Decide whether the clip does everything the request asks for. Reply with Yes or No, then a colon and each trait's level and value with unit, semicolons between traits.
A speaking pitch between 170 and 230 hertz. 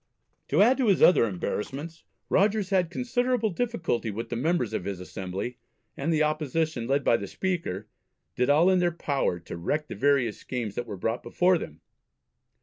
No: medium, 145 Hz